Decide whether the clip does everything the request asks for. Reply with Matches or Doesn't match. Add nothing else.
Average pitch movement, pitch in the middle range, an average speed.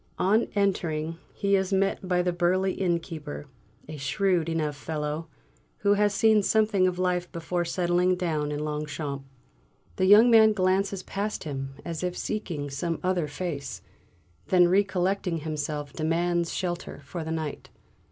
Matches